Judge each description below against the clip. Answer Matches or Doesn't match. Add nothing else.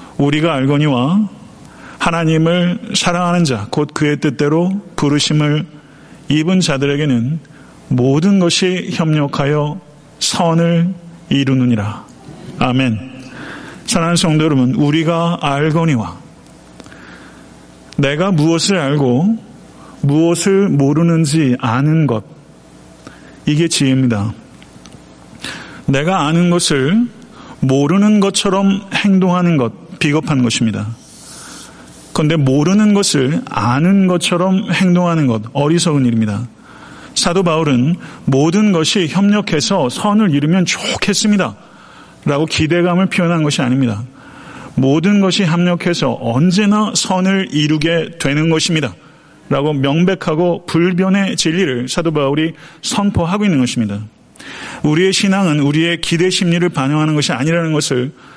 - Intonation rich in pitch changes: Doesn't match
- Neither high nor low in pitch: Matches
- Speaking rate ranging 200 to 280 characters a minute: Matches